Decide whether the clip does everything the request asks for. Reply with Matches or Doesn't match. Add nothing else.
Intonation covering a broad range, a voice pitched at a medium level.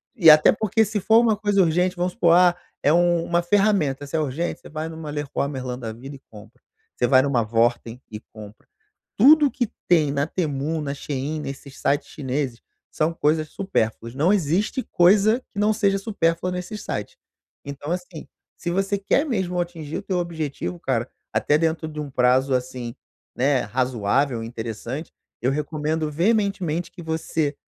Doesn't match